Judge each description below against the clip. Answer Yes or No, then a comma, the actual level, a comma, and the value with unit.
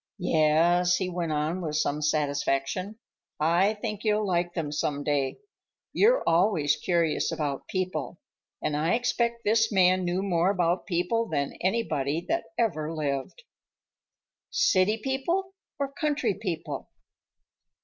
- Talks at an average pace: No, slow, 130 wpm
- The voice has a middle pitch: Yes, medium, 180 Hz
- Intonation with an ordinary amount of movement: No, wide, 5.8 semitones